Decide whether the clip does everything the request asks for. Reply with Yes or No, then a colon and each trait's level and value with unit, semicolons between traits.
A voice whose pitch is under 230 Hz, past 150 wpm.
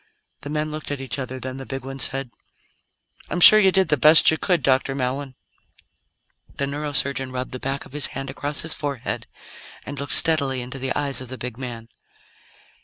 Yes: low, 135 Hz; average, 195 wpm